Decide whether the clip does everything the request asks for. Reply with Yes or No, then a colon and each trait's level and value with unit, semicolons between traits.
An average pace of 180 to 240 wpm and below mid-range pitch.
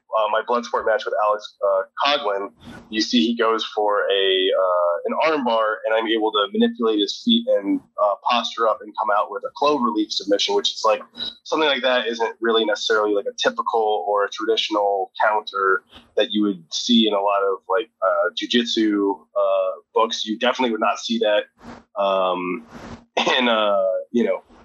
Yes: average, 190 wpm; low, 110 Hz